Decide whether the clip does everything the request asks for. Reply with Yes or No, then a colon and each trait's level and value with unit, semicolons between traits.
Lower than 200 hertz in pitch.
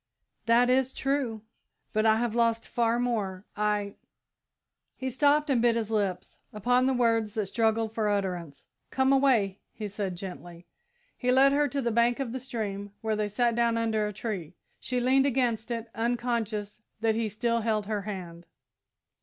No: high, 225 Hz